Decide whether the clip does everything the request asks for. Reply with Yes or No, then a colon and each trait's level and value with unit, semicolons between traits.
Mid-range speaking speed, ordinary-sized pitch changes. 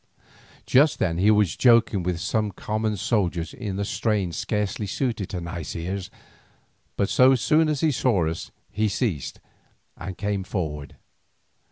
Yes: average, 150 wpm; average, 4.2 semitones